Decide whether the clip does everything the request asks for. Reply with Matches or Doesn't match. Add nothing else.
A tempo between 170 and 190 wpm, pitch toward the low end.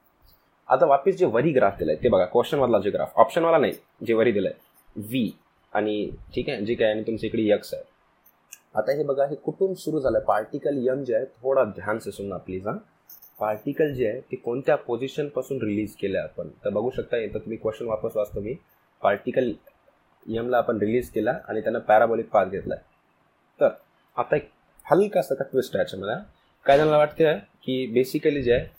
Matches